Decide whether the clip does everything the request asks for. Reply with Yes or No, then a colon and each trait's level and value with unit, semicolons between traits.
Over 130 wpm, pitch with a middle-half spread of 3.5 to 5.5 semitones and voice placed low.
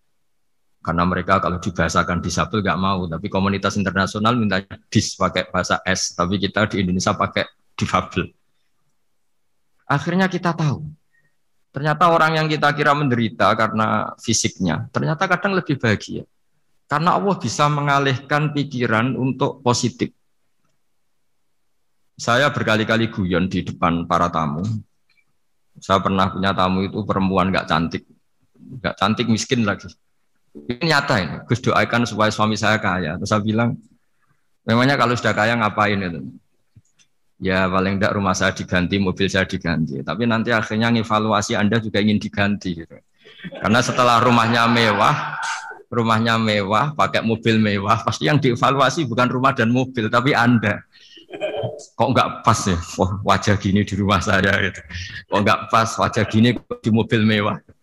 Yes: fast, 140 wpm; average, 3.9 semitones; low, 110 Hz